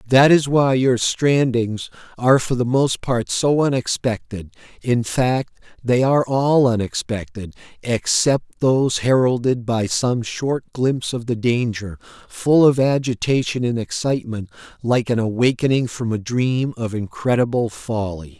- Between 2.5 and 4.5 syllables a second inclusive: Yes, 4.3 syllables/s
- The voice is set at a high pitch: No, low, 120 Hz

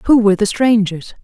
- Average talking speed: Yes, average, 195 wpm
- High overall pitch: Yes, high, 210 Hz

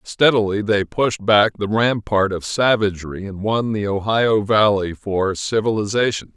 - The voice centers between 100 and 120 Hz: Yes, low, 105 Hz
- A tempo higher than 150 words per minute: No, average, 140 wpm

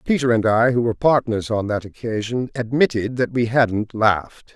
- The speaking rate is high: No, average, 185 wpm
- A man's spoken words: Yes, male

